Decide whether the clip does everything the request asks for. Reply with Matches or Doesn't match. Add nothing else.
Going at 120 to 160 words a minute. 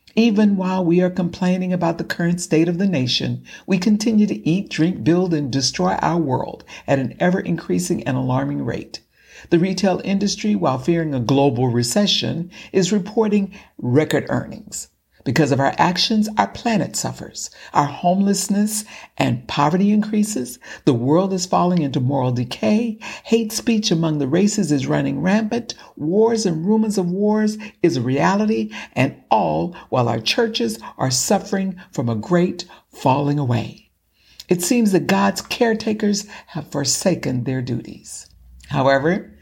Matches